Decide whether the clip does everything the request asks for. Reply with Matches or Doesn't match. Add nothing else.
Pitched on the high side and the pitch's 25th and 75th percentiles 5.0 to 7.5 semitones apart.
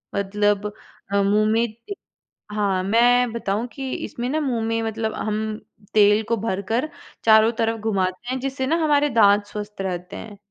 Doesn't match